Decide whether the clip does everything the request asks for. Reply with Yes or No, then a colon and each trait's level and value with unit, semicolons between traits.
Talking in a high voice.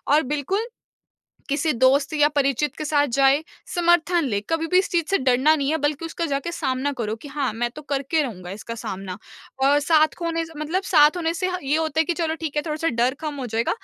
Yes: very high, 295 Hz